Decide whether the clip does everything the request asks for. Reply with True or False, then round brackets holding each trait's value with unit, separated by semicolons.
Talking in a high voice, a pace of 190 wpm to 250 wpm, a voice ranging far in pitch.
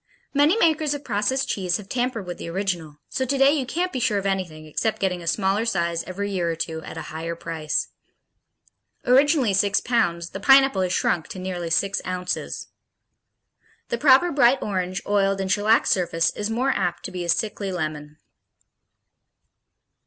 False (195 Hz; 175 wpm; 6.0 semitones)